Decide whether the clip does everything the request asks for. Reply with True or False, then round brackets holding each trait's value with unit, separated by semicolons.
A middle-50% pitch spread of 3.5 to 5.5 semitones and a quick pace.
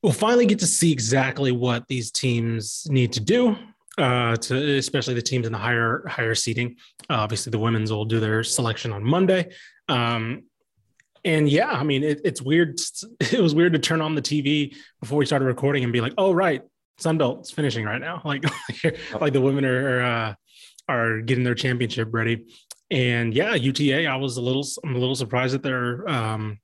False (4.2 semitones; 195 wpm)